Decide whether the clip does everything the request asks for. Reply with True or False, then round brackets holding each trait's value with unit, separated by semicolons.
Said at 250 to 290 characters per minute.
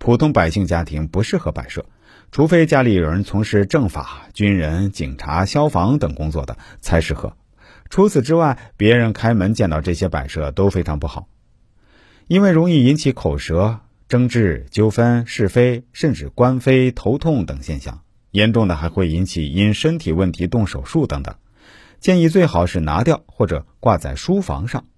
True (255 characters per minute)